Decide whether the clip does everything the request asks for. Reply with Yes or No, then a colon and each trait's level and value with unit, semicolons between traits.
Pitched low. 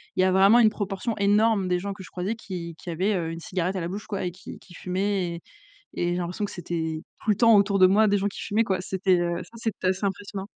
No: high, 190 Hz